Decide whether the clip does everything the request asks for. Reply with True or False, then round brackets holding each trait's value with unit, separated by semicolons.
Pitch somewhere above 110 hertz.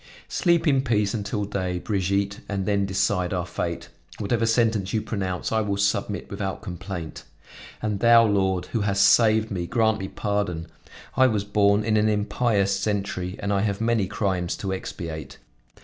False (100 Hz)